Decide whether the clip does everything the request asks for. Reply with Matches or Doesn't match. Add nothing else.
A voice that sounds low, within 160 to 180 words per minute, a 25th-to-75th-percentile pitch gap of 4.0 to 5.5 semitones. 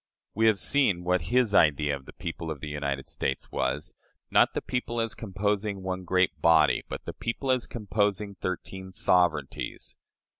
Matches